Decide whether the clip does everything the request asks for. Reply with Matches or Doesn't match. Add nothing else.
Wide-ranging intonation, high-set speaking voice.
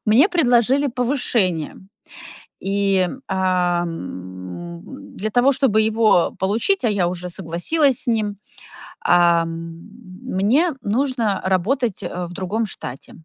Matches